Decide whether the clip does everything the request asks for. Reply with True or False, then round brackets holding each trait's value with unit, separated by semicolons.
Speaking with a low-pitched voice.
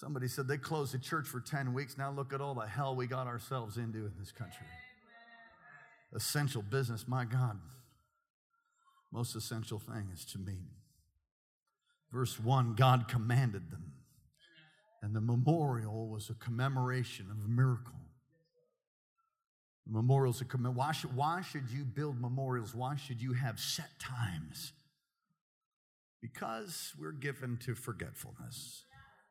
True (130 Hz)